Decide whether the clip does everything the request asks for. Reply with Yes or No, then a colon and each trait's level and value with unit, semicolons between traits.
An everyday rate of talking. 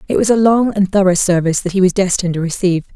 No: fast, 265 wpm